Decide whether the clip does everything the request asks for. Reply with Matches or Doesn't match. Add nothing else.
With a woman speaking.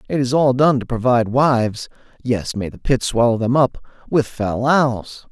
Doesn't match